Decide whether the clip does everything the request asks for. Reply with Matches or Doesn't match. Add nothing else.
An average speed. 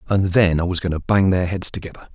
Doesn't match